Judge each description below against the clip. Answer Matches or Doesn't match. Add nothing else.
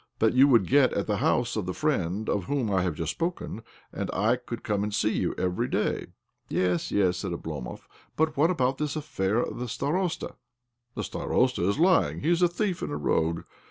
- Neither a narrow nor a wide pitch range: Doesn't match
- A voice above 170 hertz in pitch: Doesn't match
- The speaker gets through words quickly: Matches